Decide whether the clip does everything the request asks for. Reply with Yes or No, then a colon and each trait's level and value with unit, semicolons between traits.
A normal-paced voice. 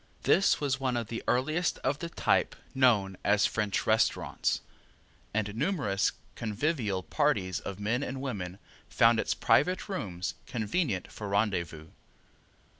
No: slow, 130 wpm